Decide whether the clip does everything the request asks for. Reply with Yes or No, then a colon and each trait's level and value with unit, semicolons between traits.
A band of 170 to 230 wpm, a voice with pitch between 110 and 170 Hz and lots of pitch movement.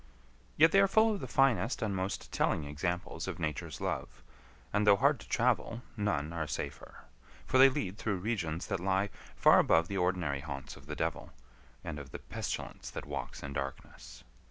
No: average, 185 wpm; very low, 90 Hz; wide, 6.5 semitones